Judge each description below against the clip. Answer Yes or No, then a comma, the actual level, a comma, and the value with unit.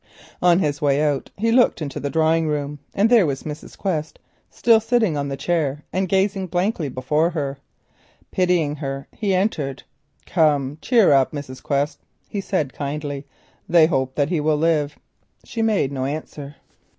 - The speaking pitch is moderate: Yes, medium, 155 Hz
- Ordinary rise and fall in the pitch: Yes, average, 4.4 semitones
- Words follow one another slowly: No, average, 165 wpm